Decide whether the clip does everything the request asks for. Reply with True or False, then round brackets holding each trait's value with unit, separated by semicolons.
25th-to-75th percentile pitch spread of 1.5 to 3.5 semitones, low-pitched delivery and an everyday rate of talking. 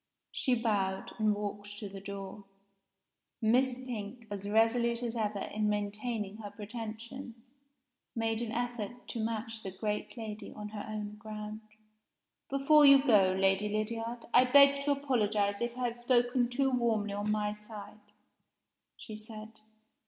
False (2.5 semitones; 220 Hz; 145 wpm)